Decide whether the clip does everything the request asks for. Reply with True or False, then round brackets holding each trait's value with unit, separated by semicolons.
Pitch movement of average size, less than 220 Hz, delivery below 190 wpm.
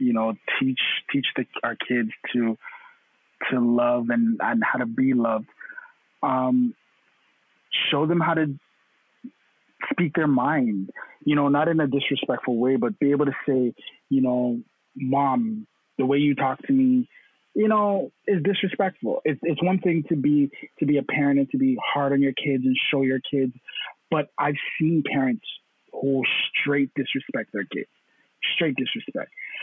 True (4.1 semitones; 140 Hz; 165 wpm)